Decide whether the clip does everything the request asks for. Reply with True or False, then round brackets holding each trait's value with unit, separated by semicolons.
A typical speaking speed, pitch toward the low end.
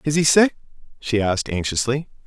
True (160 wpm; 130 Hz)